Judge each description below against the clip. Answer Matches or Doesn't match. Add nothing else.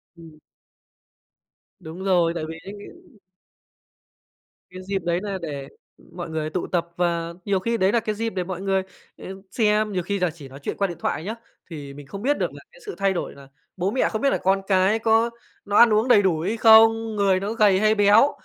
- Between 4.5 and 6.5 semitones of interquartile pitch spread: Doesn't match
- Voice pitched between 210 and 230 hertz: Doesn't match